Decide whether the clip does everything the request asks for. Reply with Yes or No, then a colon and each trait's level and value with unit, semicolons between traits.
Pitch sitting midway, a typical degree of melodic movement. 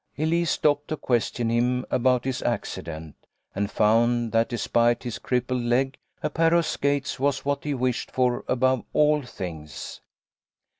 No: low, 125 Hz; average, 3.2 semitones